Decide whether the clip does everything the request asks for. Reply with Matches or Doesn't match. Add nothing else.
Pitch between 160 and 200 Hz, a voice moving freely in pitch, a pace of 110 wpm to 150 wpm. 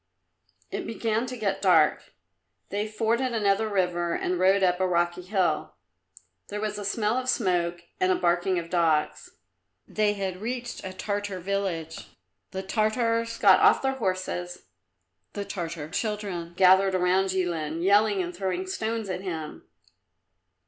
Doesn't match